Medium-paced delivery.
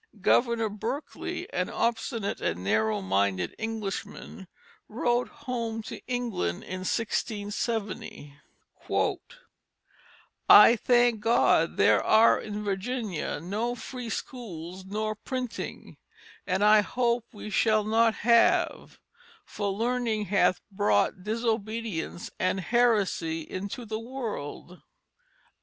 No: slow, 100 wpm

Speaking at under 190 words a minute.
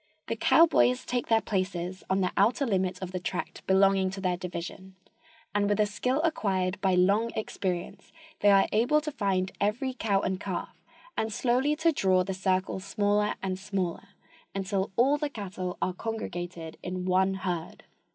Yes: average, 170 wpm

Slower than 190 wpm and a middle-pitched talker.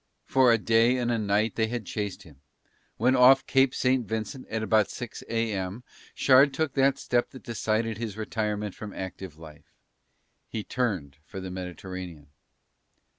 No: average, 160 wpm; low, 110 Hz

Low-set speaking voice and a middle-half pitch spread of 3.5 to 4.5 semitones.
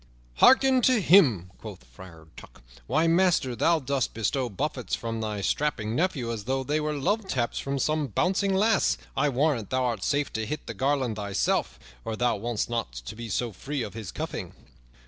No: low, 130 Hz; wide, 5.6 semitones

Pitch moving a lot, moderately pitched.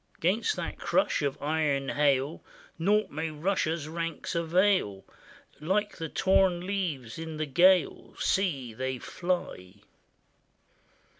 No: average, 4.5 semitones; medium, 160 Hz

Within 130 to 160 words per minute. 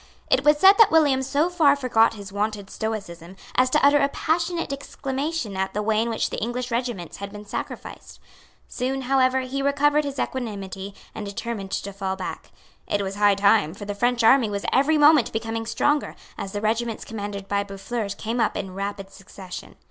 No: average, 190 wpm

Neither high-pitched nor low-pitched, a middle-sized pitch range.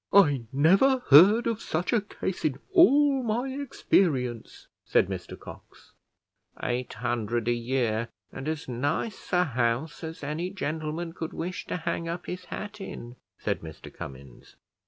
No: medium, 160 Hz; wide, 8.0 semitones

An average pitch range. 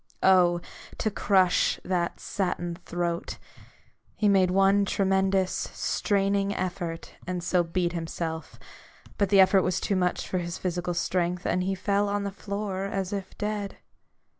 No: narrow, 2.1 semitones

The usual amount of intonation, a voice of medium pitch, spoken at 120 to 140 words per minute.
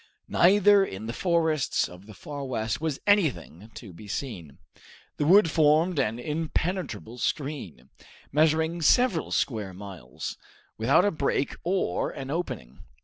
No: wide, 7.7 semitones; medium, 145 Hz; slow, 135 wpm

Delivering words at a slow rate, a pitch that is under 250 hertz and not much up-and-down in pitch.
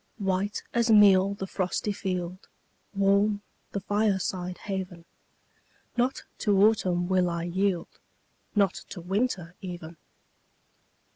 Yes: slow, 110 wpm; high, 190 Hz; narrow, 2.2 semitones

